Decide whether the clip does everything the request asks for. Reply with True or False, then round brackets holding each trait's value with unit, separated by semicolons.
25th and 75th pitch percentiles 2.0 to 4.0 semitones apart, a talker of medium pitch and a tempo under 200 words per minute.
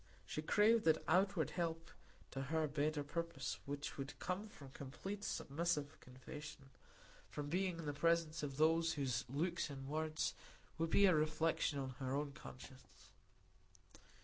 True (3.0 semitones; 155 Hz; 150 wpm)